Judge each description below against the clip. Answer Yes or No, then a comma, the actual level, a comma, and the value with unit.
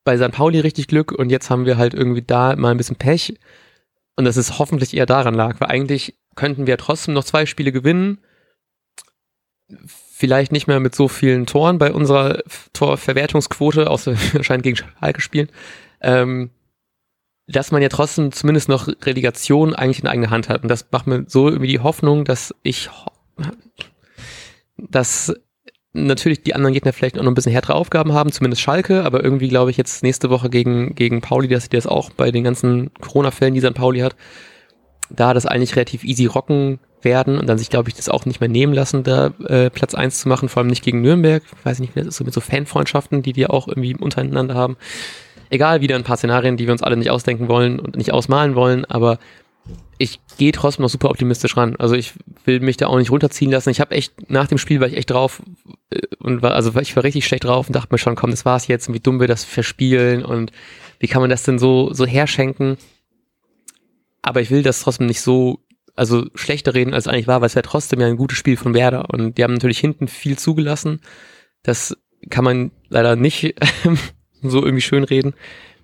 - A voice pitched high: No, low, 130 Hz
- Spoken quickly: Yes, fast, 210 wpm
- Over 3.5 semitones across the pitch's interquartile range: No, narrow, 2.5 semitones